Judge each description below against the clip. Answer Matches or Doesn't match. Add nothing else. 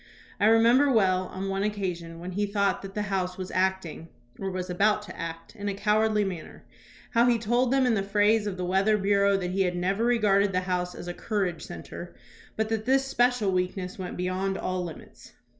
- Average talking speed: Doesn't match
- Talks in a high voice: Matches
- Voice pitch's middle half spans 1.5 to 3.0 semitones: Matches